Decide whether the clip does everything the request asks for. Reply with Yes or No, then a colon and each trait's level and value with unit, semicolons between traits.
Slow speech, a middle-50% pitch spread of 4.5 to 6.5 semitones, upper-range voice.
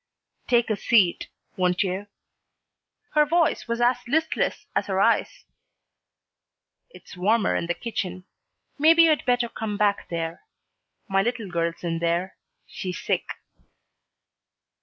Yes: slow, 125 wpm; average, 5.2 semitones; high, 205 Hz